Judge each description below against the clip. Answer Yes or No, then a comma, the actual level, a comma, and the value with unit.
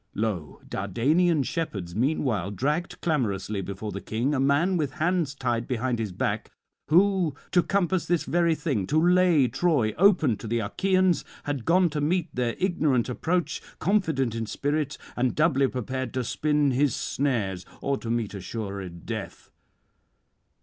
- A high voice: No, low, 135 Hz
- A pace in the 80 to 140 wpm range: No, average, 150 wpm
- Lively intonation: Yes, wide, 6.6 semitones